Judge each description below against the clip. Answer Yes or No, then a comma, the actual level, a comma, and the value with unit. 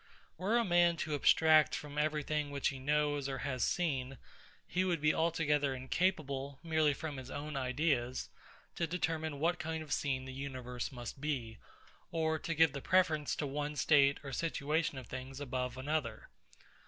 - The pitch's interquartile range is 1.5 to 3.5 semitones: Yes, average, 3.0 semitones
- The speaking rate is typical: Yes, average, 170 wpm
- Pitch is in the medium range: Yes, medium, 145 Hz